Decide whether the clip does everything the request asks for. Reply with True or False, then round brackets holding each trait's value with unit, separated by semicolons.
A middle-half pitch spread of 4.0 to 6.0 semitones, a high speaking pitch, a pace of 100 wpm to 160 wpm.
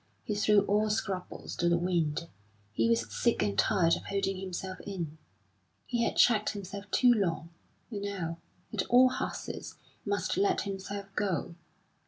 False (3.3 semitones; 195 Hz; 155 wpm)